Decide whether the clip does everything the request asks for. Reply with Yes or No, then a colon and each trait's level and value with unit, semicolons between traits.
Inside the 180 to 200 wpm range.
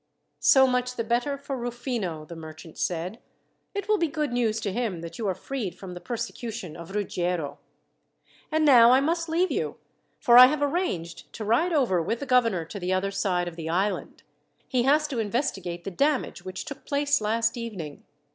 Yes: average, 195 wpm